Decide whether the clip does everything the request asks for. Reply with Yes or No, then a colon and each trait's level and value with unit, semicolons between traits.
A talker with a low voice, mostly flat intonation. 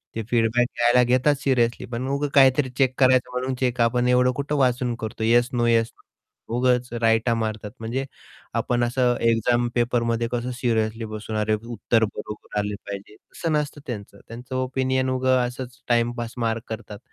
Yes: low, 120 Hz; narrow, 2.0 semitones